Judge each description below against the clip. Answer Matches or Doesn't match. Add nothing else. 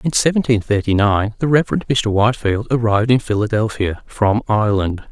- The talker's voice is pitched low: Matches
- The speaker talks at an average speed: Matches